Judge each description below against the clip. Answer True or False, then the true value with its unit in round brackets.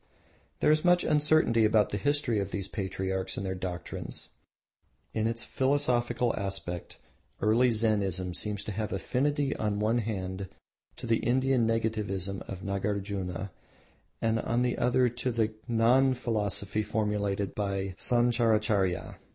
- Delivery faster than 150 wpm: False (135 wpm)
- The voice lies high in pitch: False (110 Hz)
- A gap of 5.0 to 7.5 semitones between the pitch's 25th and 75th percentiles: False (3.6 semitones)